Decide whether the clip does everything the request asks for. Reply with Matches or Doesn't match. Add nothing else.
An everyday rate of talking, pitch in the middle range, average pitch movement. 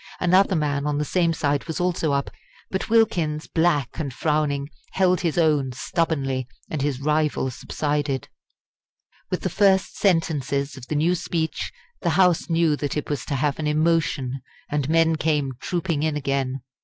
Matches